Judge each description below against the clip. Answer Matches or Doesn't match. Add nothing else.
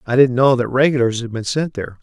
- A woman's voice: Doesn't match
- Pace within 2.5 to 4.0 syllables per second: Doesn't match